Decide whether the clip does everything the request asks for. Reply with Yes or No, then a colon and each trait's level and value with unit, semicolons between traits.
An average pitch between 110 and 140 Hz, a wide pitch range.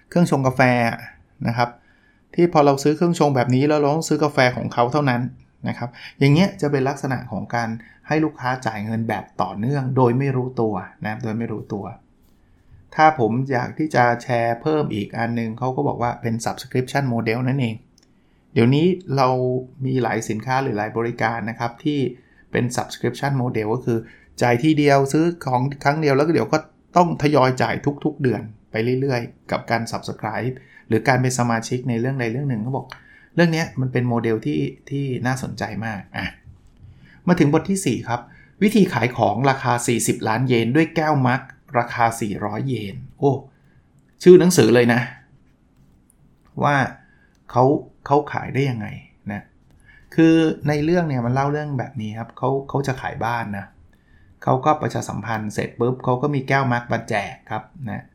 No: low, 125 Hz; average, 3.6 semitones